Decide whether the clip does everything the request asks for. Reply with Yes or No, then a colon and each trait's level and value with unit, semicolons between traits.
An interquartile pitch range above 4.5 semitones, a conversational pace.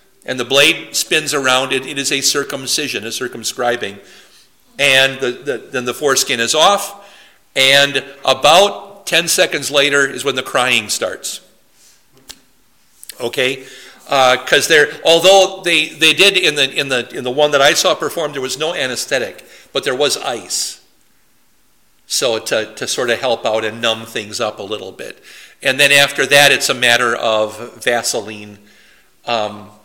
Yes: average, 5.0 semitones; average, 160 wpm